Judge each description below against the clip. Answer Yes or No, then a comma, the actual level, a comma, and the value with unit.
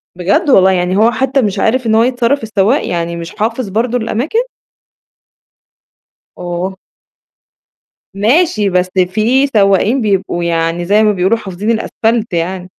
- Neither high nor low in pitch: No, high, 210 Hz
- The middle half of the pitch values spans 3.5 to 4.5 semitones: Yes, average, 4.2 semitones